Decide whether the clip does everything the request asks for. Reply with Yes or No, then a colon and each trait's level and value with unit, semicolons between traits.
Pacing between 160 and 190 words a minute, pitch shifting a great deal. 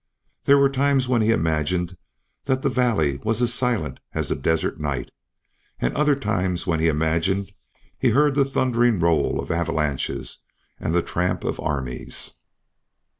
No: average, 150 wpm; wide, 7.9 semitones